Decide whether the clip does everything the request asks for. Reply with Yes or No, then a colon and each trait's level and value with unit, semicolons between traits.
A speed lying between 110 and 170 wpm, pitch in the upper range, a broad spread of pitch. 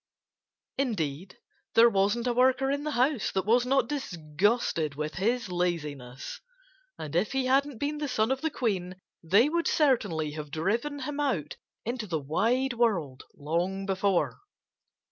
Yes: average, 150 wpm; high, 215 Hz; wide, 7.6 semitones